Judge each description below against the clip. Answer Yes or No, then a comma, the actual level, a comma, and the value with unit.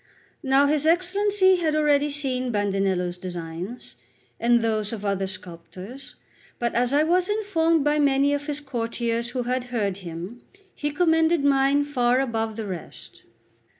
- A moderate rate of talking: Yes, average, 150 wpm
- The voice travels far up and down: Yes, wide, 5.8 semitones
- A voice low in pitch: No, very high, 255 Hz